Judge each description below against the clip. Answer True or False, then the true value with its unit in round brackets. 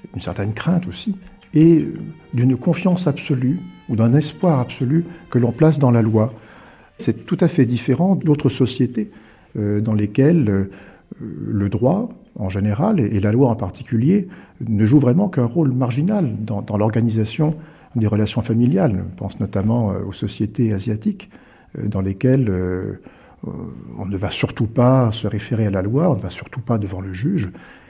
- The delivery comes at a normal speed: True (170 wpm)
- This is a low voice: True (120 Hz)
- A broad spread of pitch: True (6.5 semitones)